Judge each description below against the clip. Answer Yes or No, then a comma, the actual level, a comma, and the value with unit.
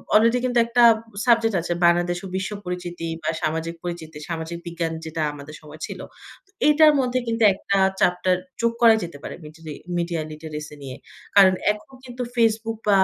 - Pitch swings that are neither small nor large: No, wide, 5.9 semitones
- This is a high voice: No, medium, 175 Hz